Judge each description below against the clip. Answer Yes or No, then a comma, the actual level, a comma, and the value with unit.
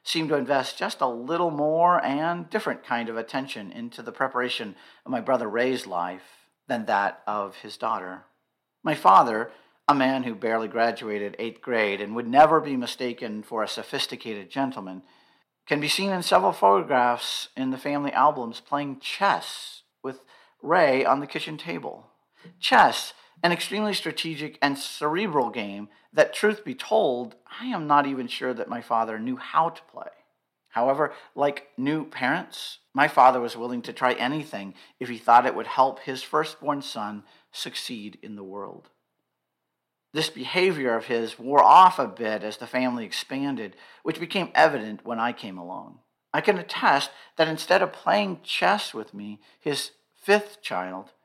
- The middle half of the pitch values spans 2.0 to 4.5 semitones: No, average, 5.2 semitones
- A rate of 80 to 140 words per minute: No, average, 165 wpm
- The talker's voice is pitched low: Yes, low, 130 Hz